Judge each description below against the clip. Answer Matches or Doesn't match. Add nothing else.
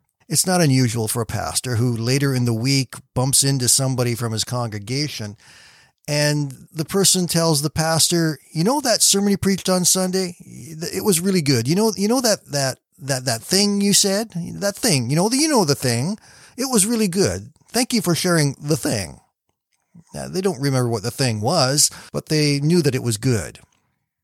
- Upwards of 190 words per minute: Matches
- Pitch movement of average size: Doesn't match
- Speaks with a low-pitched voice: Doesn't match